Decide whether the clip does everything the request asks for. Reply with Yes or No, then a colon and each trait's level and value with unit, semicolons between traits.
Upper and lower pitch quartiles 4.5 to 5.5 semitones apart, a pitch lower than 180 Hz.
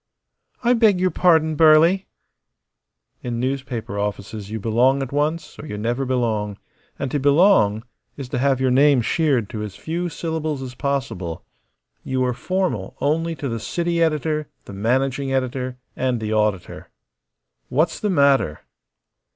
Yes: average, 5.2 semitones; low, 135 Hz